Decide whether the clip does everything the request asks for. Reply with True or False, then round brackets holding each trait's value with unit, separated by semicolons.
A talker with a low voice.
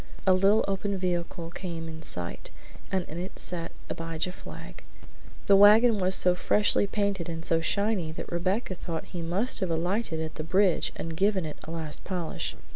False (180 Hz)